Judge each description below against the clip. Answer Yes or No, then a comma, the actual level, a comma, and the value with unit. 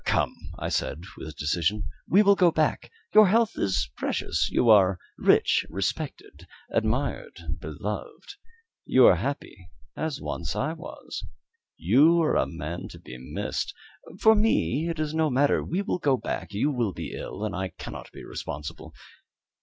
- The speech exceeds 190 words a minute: No, average, 160 wpm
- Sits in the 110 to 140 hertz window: Yes, low, 135 Hz